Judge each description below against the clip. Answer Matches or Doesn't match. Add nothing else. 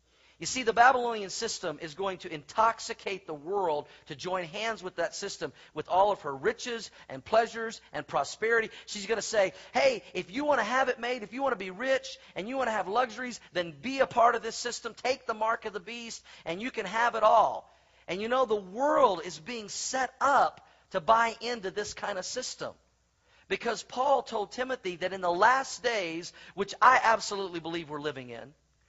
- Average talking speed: Doesn't match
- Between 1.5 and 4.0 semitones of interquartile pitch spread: Doesn't match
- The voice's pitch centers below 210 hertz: Doesn't match